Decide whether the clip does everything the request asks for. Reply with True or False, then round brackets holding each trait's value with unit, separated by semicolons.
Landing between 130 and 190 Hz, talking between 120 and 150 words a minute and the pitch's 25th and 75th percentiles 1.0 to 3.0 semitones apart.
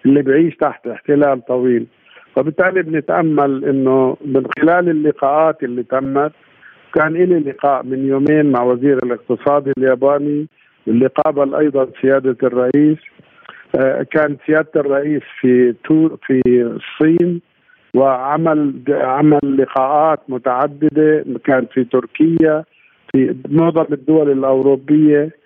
False (140 Hz; 105 wpm; 2.7 semitones)